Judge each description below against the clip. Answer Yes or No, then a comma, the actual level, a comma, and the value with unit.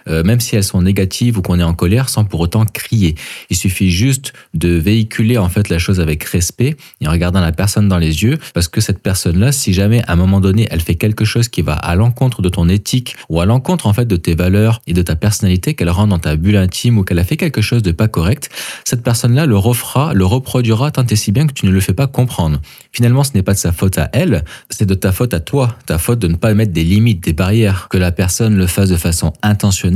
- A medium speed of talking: No, fast, 260 wpm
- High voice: No, low, 100 Hz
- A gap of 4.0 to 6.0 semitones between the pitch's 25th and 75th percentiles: Yes, average, 4.8 semitones